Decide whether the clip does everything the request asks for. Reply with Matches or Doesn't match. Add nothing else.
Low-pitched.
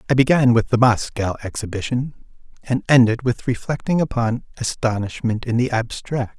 Matches